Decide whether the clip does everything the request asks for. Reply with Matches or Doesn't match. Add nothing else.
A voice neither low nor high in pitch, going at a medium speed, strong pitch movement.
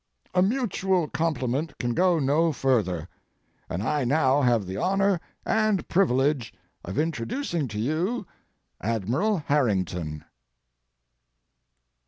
Doesn't match